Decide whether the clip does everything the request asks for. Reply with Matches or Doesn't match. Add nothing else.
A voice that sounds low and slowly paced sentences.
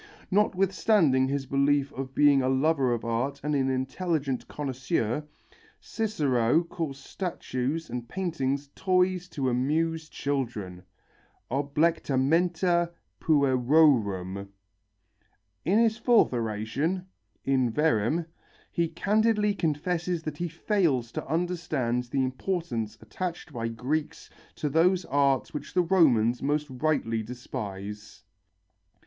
Doesn't match